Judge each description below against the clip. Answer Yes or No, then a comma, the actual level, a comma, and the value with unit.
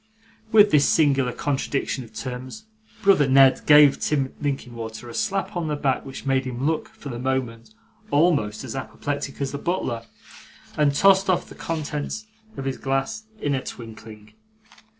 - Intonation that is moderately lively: Yes, average, 3.0 semitones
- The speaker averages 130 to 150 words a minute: No, average, 160 wpm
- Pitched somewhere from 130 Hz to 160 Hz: Yes, medium, 140 Hz